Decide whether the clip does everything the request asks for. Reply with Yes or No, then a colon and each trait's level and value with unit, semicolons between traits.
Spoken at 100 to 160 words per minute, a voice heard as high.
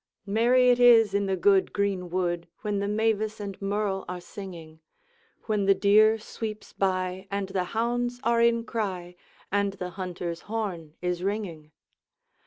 Yes: average, 150 wpm; high, 200 Hz